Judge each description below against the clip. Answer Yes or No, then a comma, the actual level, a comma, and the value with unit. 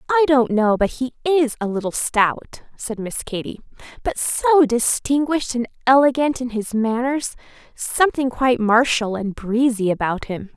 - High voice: Yes, high, 245 Hz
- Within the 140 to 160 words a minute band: Yes, average, 150 wpm